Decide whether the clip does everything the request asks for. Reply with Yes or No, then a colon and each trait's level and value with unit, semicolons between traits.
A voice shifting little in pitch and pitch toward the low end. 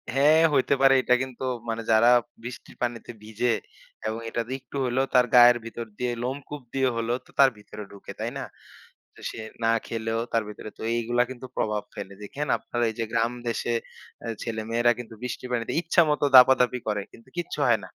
Yes: narrow, 2.3 semitones; low, 120 Hz